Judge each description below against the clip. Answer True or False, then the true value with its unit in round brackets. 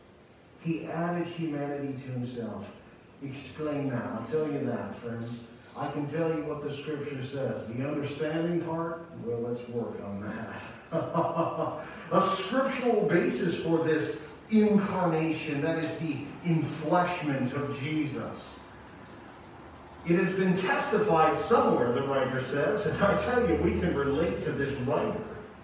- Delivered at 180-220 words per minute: False (135 wpm)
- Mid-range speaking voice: True (155 Hz)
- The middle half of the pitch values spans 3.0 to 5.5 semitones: True (3.4 semitones)